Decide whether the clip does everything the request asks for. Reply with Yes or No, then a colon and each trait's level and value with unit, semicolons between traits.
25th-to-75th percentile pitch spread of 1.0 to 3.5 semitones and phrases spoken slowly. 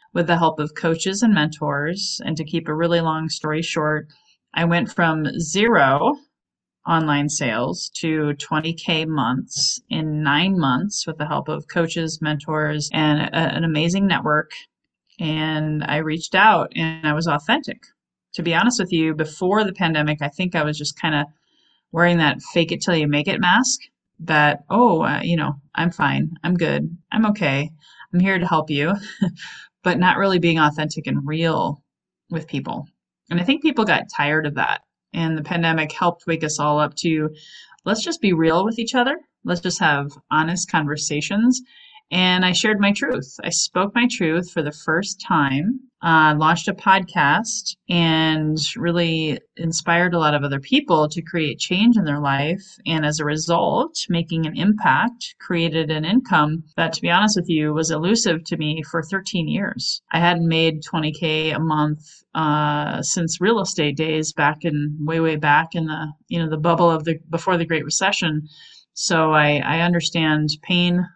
No: average, 3.2 semitones; average, 180 wpm